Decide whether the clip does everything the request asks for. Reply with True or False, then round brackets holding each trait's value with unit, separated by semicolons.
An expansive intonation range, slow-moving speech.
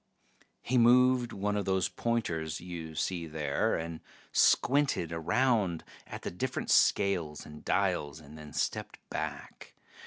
True (6.8 semitones; 130 wpm)